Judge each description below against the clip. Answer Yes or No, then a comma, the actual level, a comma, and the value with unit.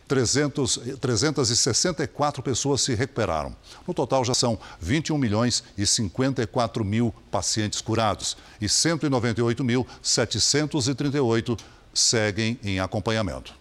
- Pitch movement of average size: Yes, average, 4.1 semitones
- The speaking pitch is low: Yes, low, 120 Hz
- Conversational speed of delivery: No, slow, 90 wpm